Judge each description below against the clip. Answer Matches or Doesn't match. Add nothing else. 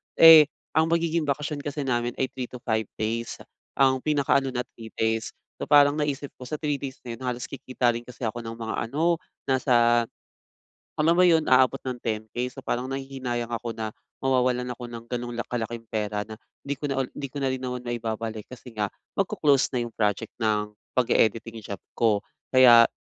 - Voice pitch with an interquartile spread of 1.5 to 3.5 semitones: Matches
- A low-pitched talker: Matches